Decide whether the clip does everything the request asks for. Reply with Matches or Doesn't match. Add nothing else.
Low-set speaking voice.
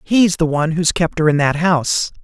Doesn't match